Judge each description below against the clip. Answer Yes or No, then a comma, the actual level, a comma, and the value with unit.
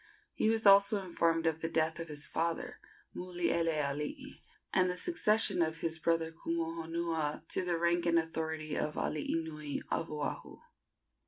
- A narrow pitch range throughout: Yes, narrow, 1.3 semitones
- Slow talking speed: No, average, 150 wpm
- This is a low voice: No, medium, 165 Hz